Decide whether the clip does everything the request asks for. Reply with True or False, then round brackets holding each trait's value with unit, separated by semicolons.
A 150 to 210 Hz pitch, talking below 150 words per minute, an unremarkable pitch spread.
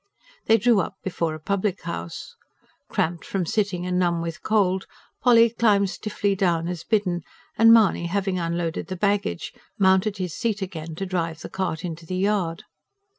False (185 Hz; 175 wpm; 3.2 semitones)